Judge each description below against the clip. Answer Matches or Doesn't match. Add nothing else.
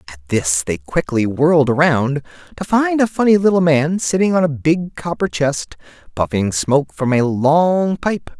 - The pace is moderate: Matches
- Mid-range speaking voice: Matches